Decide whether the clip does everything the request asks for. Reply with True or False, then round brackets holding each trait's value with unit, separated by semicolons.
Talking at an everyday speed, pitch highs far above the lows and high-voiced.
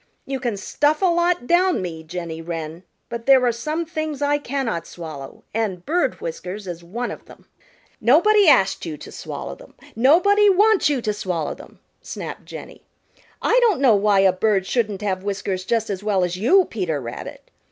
True (185 wpm; 8.8 semitones; 225 Hz)